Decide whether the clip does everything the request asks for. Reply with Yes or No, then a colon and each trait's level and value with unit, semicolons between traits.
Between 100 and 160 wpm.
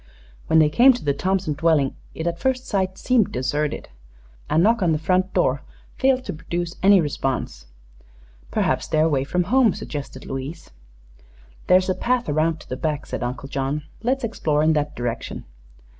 No: average, 175 wpm